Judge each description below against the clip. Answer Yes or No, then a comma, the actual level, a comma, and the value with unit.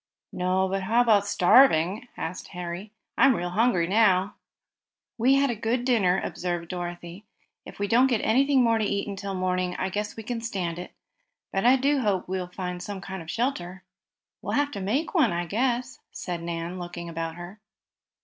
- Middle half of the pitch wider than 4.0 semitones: Yes, average, 4.7 semitones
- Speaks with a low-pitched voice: No, high, 195 Hz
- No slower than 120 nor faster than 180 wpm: No, average, 190 wpm